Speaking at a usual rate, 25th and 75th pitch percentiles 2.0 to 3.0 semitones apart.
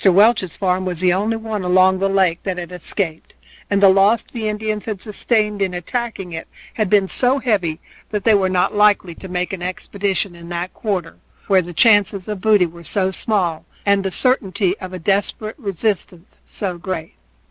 Yes: average, 190 wpm; average, 2.7 semitones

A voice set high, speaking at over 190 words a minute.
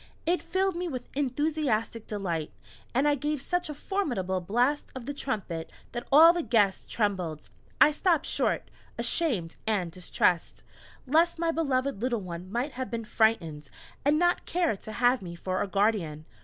No: high, 245 Hz; average, 165 wpm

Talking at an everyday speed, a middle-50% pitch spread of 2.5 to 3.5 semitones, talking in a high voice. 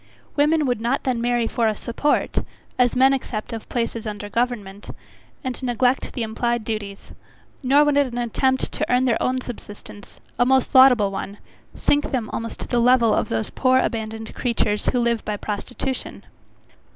Yes: average, 170 wpm; average, 2.9 semitones; high, 240 Hz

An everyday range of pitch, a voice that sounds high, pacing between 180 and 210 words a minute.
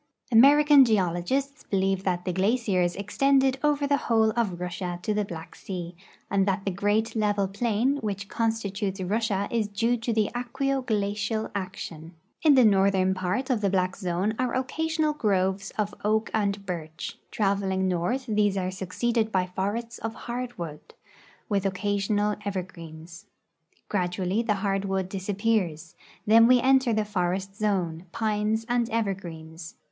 No: average, 3.5 semitones; high, 205 Hz; average, 145 wpm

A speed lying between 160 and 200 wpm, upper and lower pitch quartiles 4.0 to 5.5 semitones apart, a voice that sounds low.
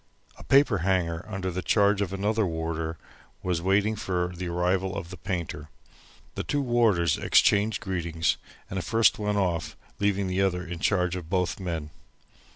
No: average, 165 wpm; average, 2.9 semitones; very low, 95 Hz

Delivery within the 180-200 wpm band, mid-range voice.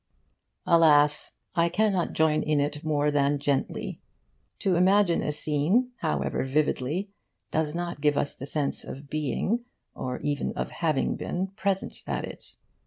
No: average, 145 wpm; medium, 155 Hz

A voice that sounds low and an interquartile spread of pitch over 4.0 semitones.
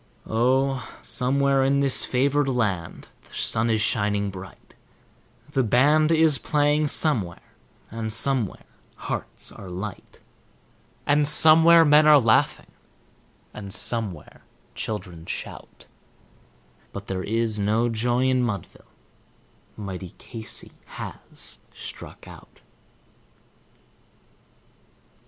Yes: low, 120 Hz; average, 5.2 semitones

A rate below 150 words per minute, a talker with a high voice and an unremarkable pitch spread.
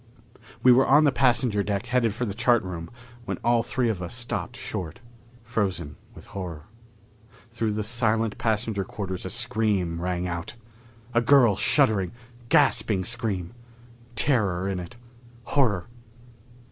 No: average, 140 wpm; low, 110 Hz; average, 4.4 semitones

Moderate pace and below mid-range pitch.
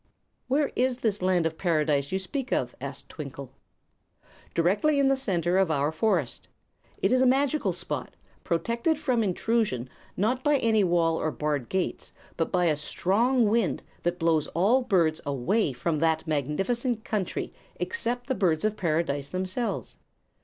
No: average, 155 wpm; medium, 185 Hz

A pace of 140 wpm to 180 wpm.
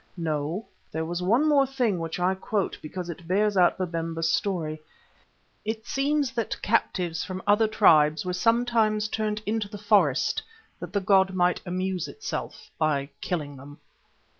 Yes: average, 155 wpm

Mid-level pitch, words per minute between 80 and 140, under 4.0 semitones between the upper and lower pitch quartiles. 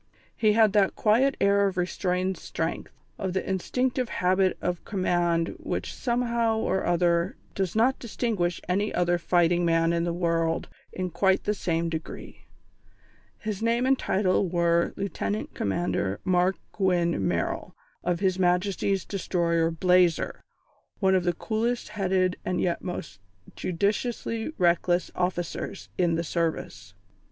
Yes: medium, 180 Hz; slow, 135 wpm; average, 2.8 semitones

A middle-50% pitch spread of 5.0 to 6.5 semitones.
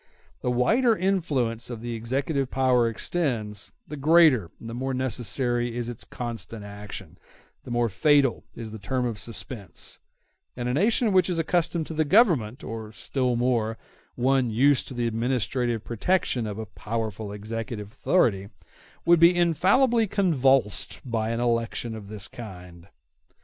No: average, 4.5 semitones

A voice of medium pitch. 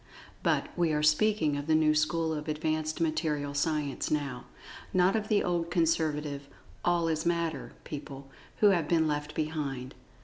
Yes: medium, 155 Hz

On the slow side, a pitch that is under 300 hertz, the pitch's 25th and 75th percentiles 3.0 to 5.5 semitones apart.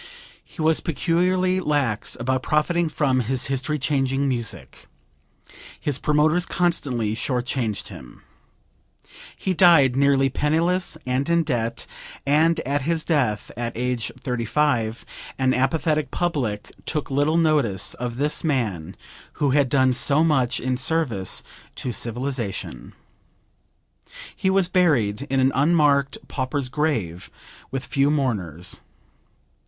Yes: slow, 120 wpm; low, 135 Hz; average, 4.1 semitones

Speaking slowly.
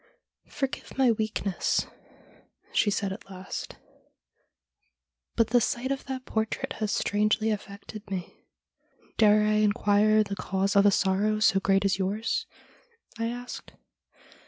No: average, 145 wpm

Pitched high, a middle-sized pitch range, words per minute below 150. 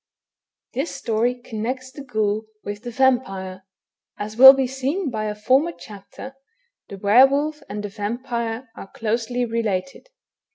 Yes: high, 235 Hz; average, 3.9 semitones; average, 140 wpm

